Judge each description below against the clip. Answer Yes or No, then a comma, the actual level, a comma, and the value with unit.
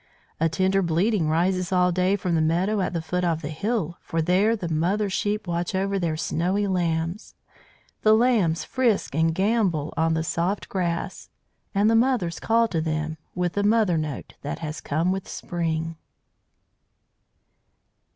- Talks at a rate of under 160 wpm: No, average, 165 wpm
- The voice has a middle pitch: Yes, medium, 180 Hz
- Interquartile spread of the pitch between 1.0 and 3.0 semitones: No, average, 3.6 semitones